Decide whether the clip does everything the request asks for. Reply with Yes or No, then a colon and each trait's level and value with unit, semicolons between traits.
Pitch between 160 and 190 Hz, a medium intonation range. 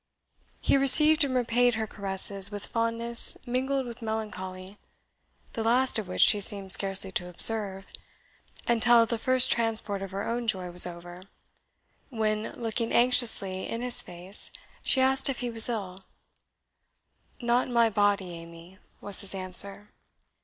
No: high, 220 Hz; average, 3.7 semitones